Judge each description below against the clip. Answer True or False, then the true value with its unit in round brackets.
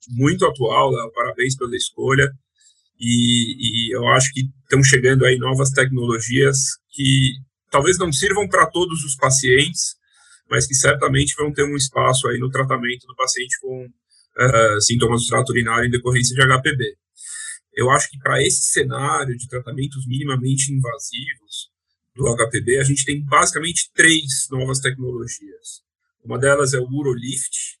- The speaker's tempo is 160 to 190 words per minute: False (145 wpm)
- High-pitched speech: False (130 Hz)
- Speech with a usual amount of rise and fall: False (2.3 semitones)